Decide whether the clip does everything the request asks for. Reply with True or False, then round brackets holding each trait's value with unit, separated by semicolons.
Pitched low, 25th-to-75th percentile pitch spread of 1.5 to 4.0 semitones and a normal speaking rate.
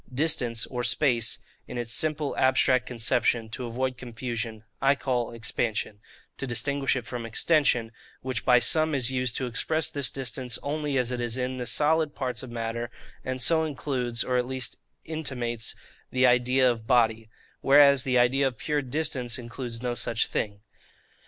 True (125 Hz; 2.4 semitones; 165 wpm)